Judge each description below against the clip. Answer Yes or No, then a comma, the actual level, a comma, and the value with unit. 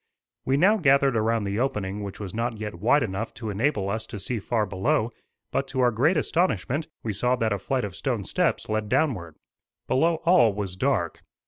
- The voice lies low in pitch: Yes, low, 115 Hz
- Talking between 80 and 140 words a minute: No, average, 200 wpm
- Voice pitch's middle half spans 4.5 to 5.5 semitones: Yes, average, 4.9 semitones